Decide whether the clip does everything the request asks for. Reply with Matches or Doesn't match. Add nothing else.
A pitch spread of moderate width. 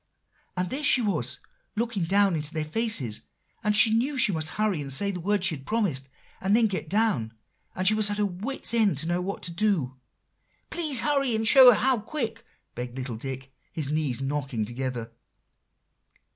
Doesn't match